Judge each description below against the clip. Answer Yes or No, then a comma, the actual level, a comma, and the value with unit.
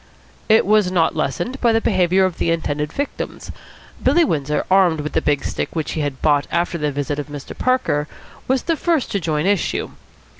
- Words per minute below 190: No, average, 195 wpm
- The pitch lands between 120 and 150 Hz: No, medium, 170 Hz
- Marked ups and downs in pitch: Yes, wide, 6.0 semitones